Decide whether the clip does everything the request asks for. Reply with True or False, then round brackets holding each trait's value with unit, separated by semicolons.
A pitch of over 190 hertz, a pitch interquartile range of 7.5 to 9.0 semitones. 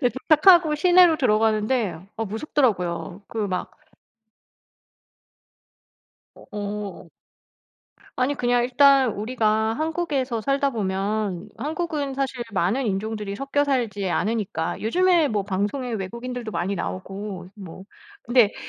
False (225 Hz; 5.2 semitones)